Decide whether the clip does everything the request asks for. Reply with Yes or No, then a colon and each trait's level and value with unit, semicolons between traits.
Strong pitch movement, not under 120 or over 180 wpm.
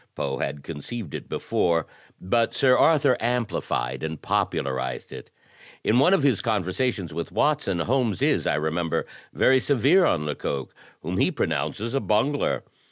Yes: wide, 8.1 semitones; average, 150 wpm